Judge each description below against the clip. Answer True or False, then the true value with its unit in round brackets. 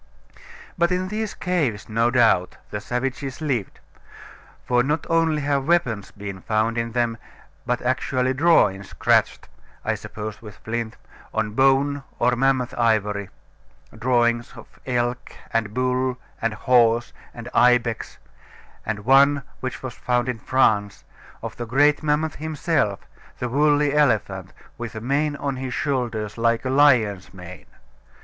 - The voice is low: True (125 Hz)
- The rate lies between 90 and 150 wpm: True (140 wpm)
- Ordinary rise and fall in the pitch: True (3.9 semitones)